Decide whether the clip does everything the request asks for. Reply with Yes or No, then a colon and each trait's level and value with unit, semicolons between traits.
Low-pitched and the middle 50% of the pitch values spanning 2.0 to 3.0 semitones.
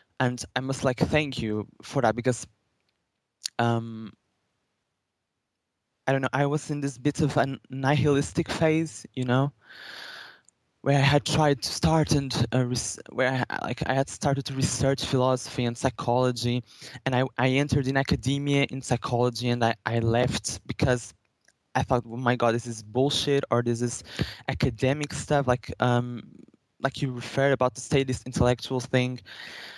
Yes: low, 130 Hz; narrow, 2.4 semitones